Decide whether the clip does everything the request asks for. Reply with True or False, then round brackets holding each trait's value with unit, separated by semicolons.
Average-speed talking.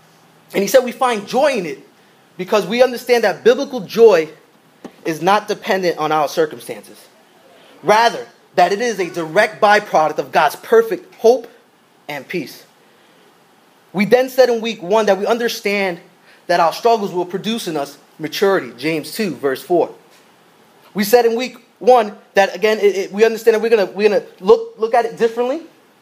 True (175 wpm)